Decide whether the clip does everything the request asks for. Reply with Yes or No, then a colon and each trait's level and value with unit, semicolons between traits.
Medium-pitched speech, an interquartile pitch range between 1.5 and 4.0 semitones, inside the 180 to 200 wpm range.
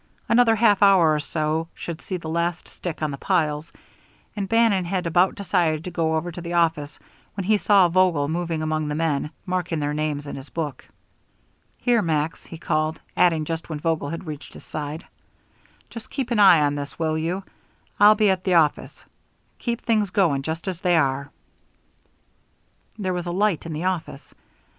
Yes: medium, 165 Hz; average, 3.3 semitones; average, 185 wpm